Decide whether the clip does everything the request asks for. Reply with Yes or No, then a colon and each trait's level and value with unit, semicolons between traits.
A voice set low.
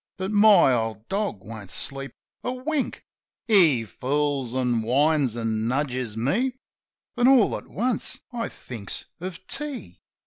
No: medium, 145 Hz